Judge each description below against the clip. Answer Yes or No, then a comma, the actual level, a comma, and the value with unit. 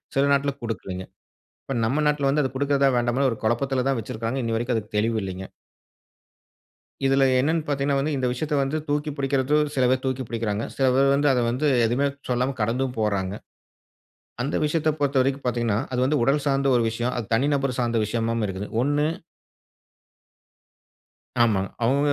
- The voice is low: Yes, low, 130 Hz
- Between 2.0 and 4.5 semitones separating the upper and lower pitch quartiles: Yes, average, 3.3 semitones